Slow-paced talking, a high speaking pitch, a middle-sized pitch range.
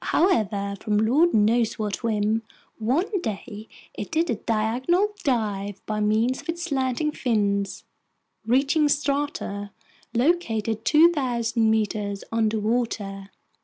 Yes: slow, 110 wpm; high, 225 Hz; average, 4.9 semitones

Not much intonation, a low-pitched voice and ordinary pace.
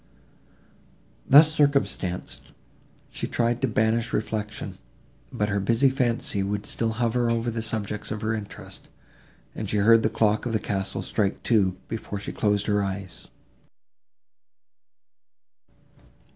No: narrow, 2.3 semitones; low, 110 Hz; slow, 130 wpm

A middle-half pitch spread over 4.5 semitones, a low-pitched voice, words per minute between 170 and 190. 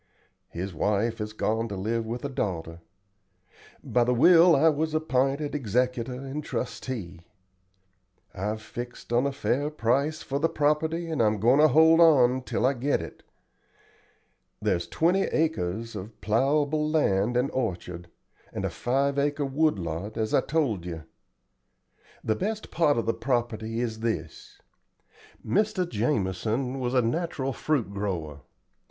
No: wide, 5.4 semitones; low, 125 Hz; average, 145 wpm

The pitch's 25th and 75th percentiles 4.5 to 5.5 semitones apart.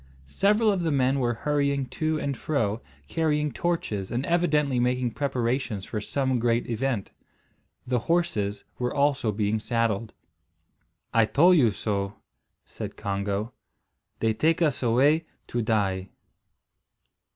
Yes: average, 5.2 semitones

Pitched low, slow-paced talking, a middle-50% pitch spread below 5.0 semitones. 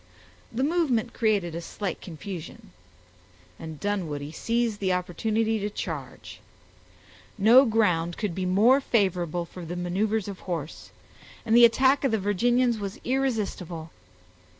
No: high, 205 Hz; slow, 130 wpm; average, 4.6 semitones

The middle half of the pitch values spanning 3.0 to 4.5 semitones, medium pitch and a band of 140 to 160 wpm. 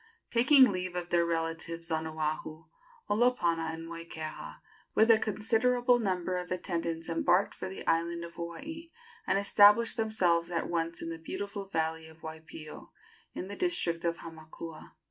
Yes: average, 3.8 semitones; medium, 170 Hz; average, 150 wpm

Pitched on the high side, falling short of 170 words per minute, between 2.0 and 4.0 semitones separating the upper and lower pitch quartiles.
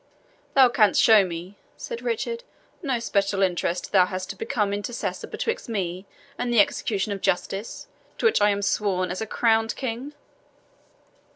Yes: high, 205 Hz; average, 160 wpm; average, 3.7 semitones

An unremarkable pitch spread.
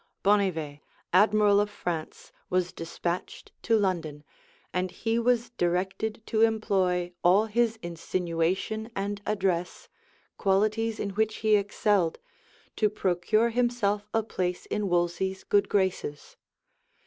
Yes: average, 3.4 semitones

